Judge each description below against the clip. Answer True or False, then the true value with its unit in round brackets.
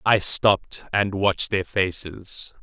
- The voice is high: False (95 Hz)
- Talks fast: False (135 wpm)